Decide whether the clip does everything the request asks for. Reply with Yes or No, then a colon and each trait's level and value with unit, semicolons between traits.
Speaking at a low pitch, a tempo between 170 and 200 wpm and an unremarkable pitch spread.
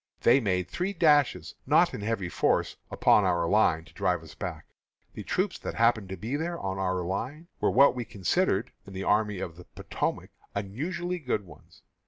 No: low, 105 Hz; average, 190 wpm; wide, 7.5 semitones